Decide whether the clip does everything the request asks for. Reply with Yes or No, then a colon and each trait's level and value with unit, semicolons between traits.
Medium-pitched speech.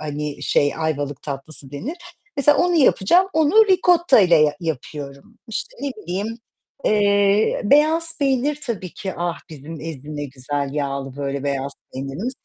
Yes: medium, 170 Hz